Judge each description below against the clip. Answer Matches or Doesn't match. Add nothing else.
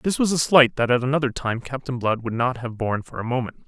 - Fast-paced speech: Matches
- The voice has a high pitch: Doesn't match